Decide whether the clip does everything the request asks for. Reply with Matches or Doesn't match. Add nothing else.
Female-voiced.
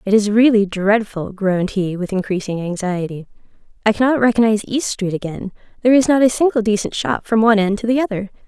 Matches